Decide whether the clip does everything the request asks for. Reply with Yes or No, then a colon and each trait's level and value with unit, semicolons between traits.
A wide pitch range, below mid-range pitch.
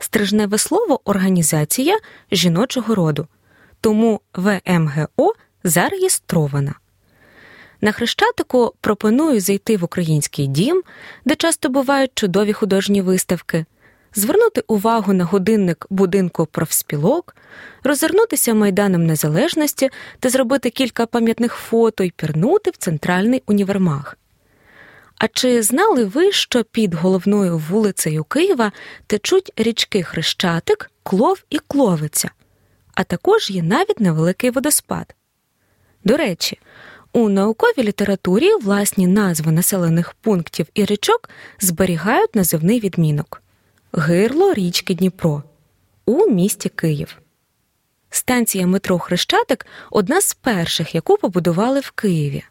No: wide, 6.0 semitones; high, 205 Hz